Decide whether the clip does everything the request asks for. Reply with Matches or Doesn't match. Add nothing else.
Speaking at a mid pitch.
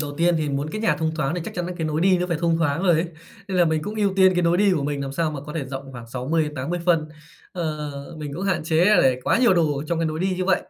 Matches